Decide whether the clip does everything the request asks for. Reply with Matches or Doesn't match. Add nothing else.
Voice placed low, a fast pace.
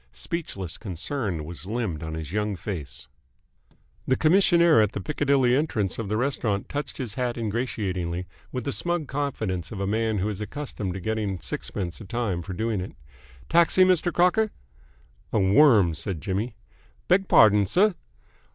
Doesn't match